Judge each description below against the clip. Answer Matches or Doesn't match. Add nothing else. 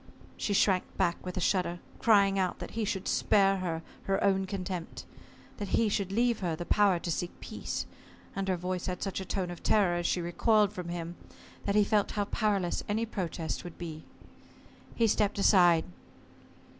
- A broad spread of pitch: Doesn't match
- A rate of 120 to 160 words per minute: Doesn't match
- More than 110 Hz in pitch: Matches